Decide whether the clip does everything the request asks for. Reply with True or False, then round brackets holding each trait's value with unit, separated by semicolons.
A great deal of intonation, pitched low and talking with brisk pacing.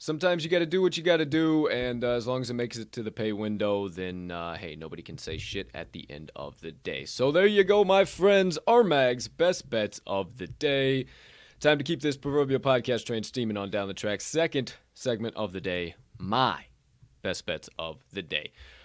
True (7.1 semitones; 125 Hz; 225 wpm)